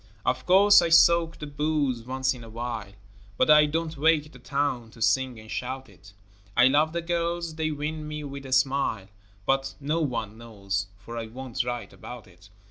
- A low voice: Yes, low, 130 Hz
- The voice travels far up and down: No, average, 4.7 semitones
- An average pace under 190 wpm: No, average, 195 wpm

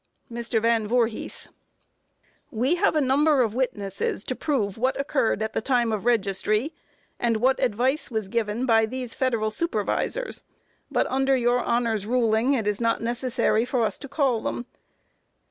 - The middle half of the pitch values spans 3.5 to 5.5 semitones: No, average, 3.0 semitones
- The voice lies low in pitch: No, high, 235 Hz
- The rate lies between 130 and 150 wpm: No, average, 160 wpm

